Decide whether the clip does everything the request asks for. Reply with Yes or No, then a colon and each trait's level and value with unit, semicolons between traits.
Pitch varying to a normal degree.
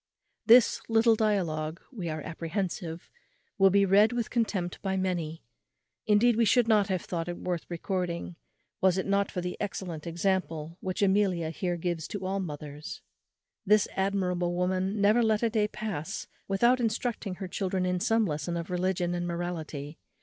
Yes: average, 3.2 semitones